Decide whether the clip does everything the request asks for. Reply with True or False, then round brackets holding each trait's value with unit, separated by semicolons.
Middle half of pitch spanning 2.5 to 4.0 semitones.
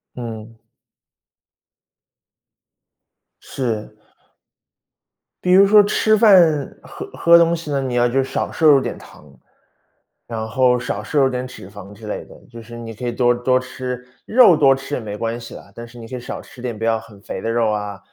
True (3.2 semitones)